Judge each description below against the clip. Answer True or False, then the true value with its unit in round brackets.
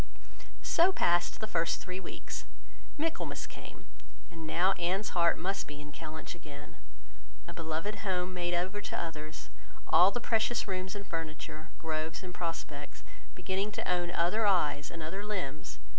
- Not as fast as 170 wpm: True (155 wpm)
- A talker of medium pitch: True (175 Hz)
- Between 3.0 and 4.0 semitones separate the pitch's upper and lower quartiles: True (3.4 semitones)